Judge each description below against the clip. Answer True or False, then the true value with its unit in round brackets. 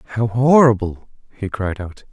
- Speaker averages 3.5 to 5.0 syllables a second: True (4.8 syllables/s)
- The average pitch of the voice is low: True (110 Hz)